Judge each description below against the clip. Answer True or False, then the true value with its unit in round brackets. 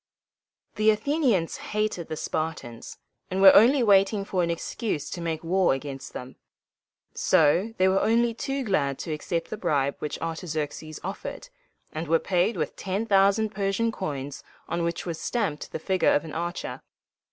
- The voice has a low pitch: False (185 Hz)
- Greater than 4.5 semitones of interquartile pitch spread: True (5.0 semitones)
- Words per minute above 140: True (165 wpm)